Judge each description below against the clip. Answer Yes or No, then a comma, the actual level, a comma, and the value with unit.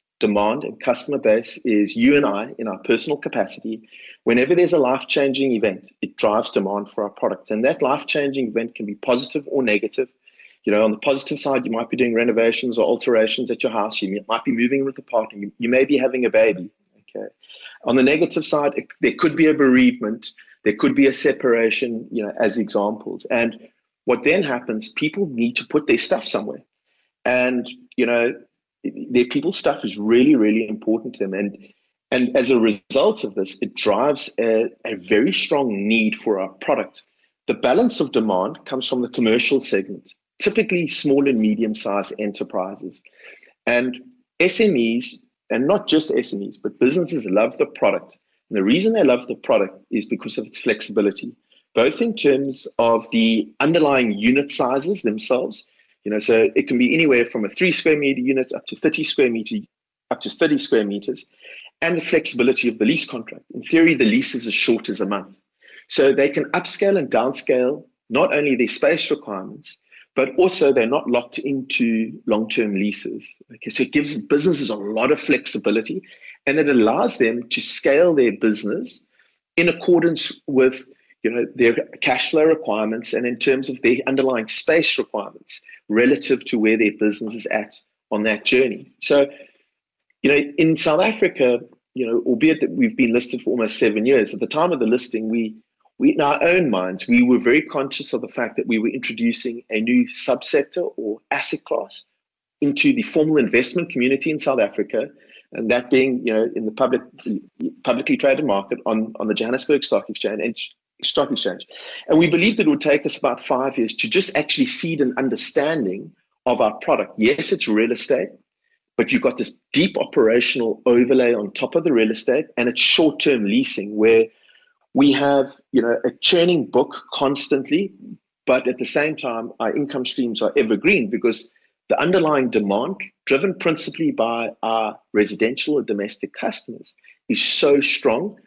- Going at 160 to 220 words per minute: Yes, average, 180 wpm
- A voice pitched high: No, low, 130 Hz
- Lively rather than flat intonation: Yes, wide, 6.2 semitones